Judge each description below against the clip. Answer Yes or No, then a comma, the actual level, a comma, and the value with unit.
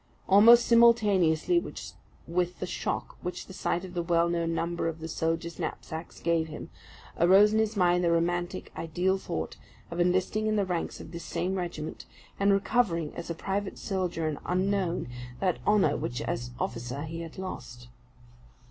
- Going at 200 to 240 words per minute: No, average, 165 wpm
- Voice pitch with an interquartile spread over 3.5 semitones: No, average, 2.7 semitones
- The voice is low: No, medium, 175 Hz